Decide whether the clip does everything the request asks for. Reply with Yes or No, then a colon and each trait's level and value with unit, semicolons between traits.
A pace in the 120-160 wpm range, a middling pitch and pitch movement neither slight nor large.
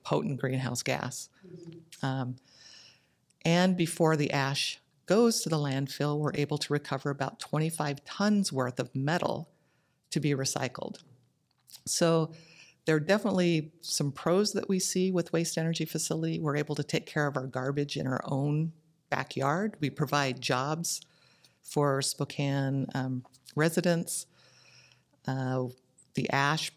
Yes: slow, 135 wpm; medium, 150 Hz; average, 3.5 semitones